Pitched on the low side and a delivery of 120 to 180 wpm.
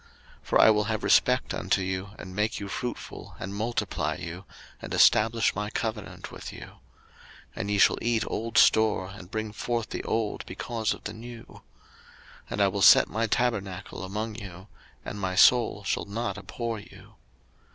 Yes: low, 105 Hz; average, 175 wpm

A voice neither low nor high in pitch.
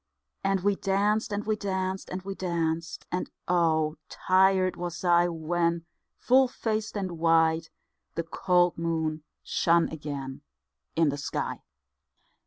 Yes: medium, 175 Hz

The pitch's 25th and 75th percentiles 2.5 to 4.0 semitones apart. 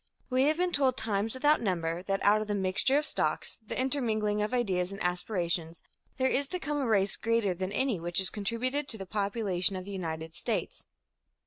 No: wide, 5.6 semitones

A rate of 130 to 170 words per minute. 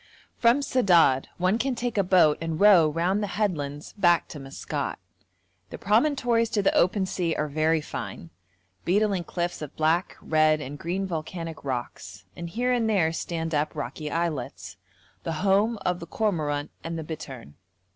Yes: average, 165 wpm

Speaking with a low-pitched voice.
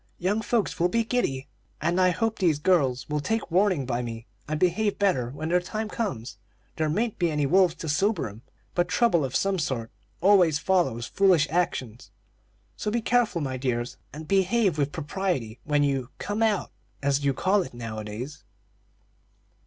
No: medium, 165 Hz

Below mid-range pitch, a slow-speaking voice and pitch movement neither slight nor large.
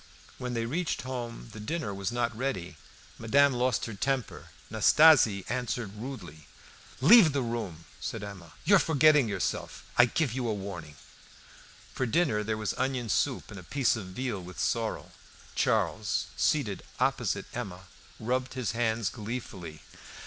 No: low, 115 Hz; average, 150 wpm; average, 4.5 semitones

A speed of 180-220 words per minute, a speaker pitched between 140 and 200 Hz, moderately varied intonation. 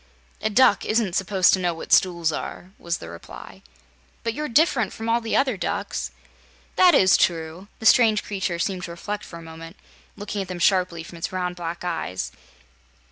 Yes: average, 185 wpm; medium, 185 Hz; average, 3.9 semitones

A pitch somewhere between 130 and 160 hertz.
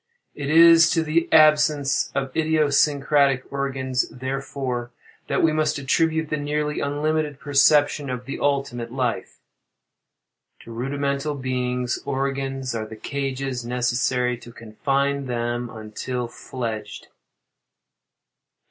Yes: low, 135 Hz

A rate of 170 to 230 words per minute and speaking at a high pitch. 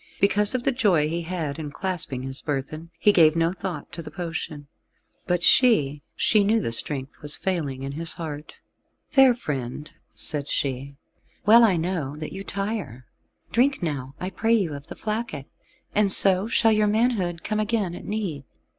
No: average, 175 wpm; medium, 170 Hz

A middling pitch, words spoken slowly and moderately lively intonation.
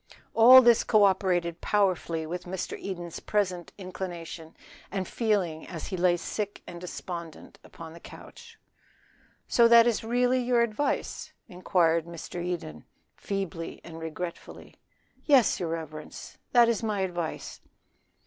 Yes: medium, 180 Hz; slow, 130 wpm; average, 4.0 semitones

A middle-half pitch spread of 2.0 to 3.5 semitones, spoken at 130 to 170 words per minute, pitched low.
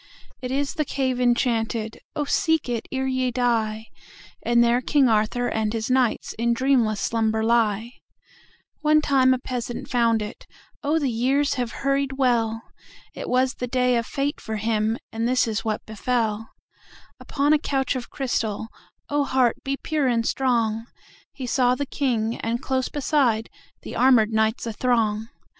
No: average, 2.9 semitones; slow, 135 wpm; high, 245 Hz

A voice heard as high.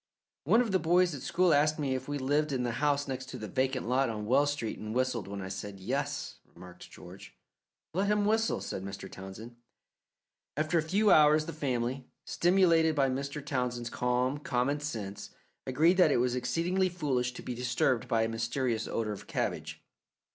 No: low, 135 Hz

